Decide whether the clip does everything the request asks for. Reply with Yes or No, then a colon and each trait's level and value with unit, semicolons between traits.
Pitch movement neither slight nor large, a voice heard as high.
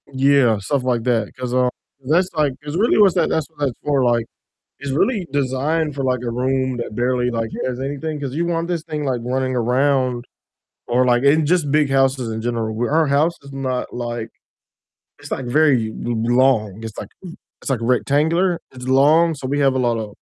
No: average, 3.2 semitones; low, 135 Hz